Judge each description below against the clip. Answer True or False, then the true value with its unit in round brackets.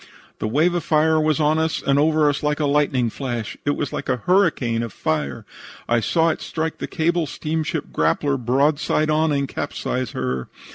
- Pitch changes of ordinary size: True (4.3 semitones)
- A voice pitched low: False (145 Hz)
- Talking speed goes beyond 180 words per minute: True (190 wpm)